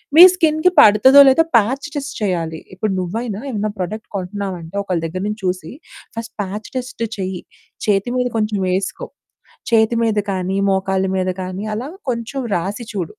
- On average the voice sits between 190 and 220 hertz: Yes, high, 205 Hz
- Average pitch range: Yes, average, 3.9 semitones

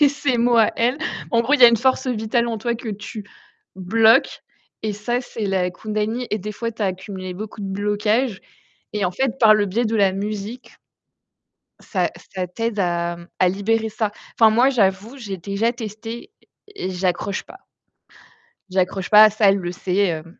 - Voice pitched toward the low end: No, high, 215 Hz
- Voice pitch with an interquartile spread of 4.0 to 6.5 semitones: No, average, 3.3 semitones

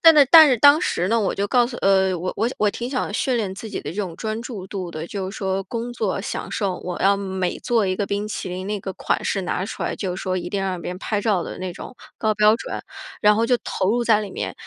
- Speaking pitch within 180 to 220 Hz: Yes, high, 200 Hz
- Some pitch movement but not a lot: Yes, average, 3.4 semitones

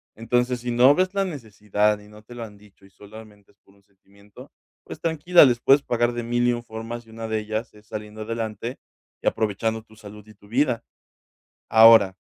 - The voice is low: Yes, low, 110 Hz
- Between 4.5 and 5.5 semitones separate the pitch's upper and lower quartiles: No, narrow, 2.4 semitones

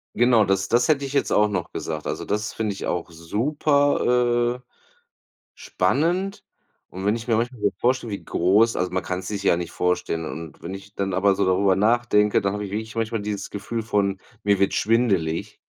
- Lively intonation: No, average, 3.8 semitones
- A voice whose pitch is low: Yes, low, 105 Hz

